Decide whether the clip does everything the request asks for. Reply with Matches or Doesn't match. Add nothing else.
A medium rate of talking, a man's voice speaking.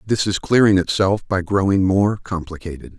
Matches